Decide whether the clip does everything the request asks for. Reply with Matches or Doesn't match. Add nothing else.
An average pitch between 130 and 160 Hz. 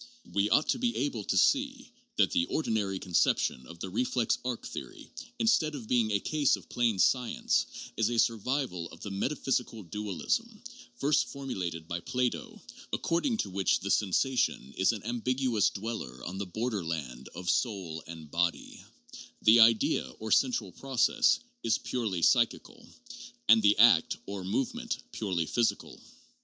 Doesn't match